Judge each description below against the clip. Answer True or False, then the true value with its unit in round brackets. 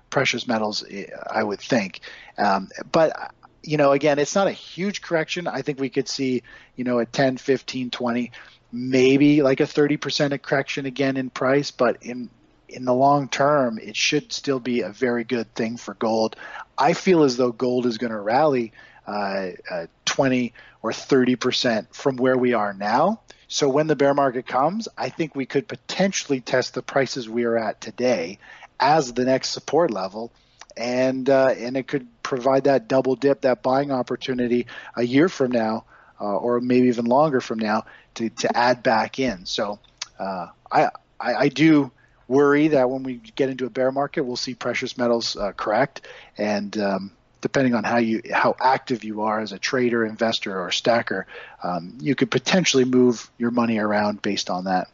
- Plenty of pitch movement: False (2.7 semitones)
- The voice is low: True (125 Hz)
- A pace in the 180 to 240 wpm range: True (185 wpm)